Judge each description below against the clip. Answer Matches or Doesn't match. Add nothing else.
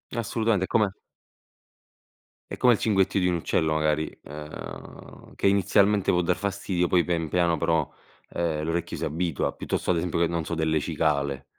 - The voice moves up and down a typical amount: Matches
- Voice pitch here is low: Matches